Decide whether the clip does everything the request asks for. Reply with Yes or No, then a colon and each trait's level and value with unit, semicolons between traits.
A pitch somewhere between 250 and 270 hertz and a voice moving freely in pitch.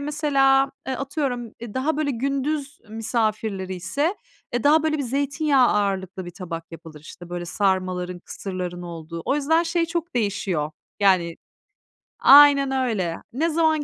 No: high, 240 Hz; wide, 7.7 semitones